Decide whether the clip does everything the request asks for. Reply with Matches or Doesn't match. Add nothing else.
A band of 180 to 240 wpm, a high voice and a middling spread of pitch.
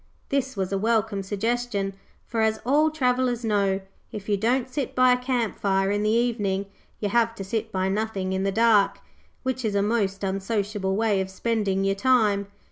Matches